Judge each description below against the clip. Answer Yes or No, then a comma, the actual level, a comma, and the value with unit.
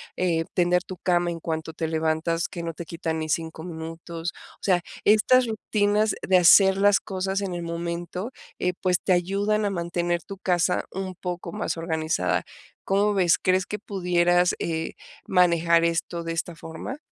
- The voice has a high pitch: No, medium, 175 Hz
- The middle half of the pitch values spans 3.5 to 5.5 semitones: No, narrow, 2.4 semitones